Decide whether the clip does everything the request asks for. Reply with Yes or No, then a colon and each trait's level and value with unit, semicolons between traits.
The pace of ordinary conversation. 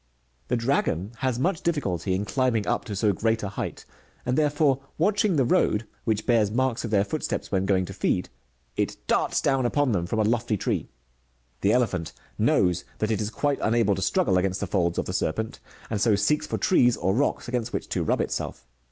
No: fast, 210 wpm